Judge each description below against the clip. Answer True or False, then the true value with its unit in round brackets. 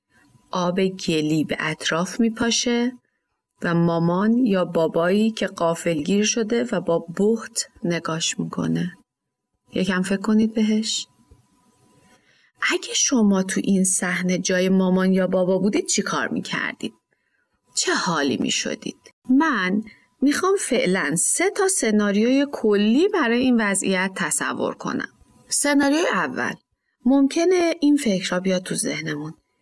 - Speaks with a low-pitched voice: False (200 Hz)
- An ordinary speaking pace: True (125 wpm)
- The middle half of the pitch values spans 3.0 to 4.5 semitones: False (5.4 semitones)